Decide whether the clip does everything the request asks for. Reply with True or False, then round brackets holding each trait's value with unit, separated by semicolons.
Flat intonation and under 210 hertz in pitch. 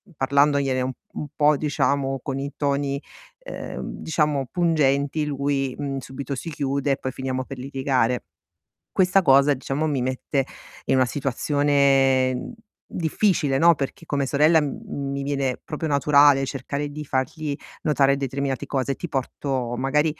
True (1.7 semitones; 140 Hz)